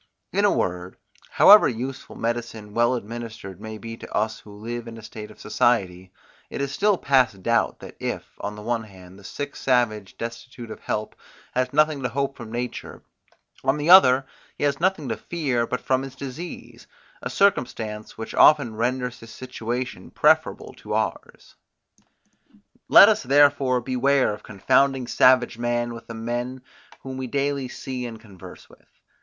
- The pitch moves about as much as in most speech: Yes, average, 3.2 semitones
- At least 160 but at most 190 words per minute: Yes, average, 170 wpm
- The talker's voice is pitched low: Yes, low, 120 Hz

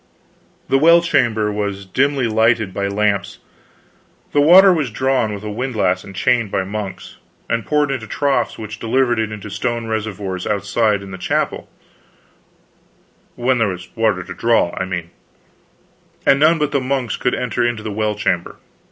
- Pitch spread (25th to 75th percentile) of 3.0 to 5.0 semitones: Yes, average, 4.2 semitones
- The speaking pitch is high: No, low, 110 Hz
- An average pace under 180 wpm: Yes, average, 160 wpm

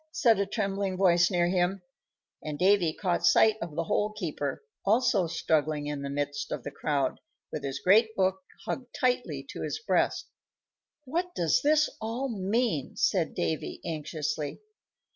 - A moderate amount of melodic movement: No, wide, 6.0 semitones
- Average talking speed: Yes, average, 155 wpm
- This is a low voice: No, medium, 185 Hz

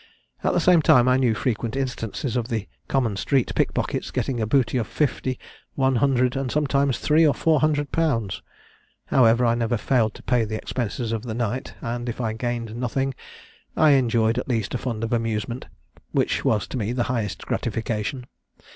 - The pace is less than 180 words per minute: No, average, 185 wpm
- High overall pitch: No, low, 120 Hz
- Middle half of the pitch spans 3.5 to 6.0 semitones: No, average, 2.8 semitones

